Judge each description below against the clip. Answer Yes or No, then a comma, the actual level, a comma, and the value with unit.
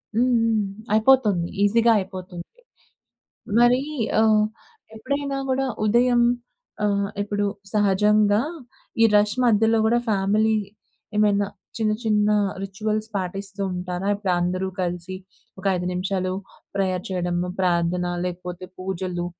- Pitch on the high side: Yes, high, 200 Hz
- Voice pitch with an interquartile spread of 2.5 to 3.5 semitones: Yes, average, 3.0 semitones